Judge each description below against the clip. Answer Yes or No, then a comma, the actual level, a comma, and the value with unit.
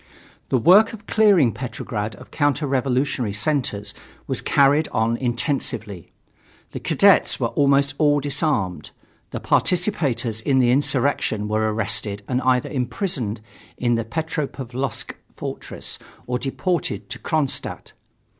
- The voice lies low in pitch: Yes, low, 130 Hz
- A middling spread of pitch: Yes, average, 4.1 semitones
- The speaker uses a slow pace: Yes, slow, 120 wpm